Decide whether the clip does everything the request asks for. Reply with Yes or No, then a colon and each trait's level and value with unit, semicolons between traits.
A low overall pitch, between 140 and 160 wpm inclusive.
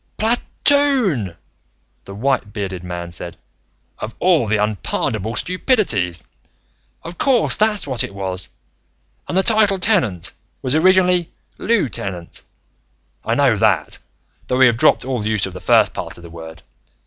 Yes: low, 120 Hz; average, 150 wpm